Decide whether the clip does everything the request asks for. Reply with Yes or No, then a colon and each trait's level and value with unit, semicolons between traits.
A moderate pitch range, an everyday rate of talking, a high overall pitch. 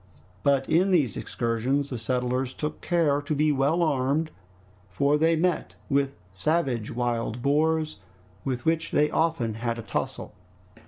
No: average, 4.4 semitones; average, 145 wpm; medium, 140 Hz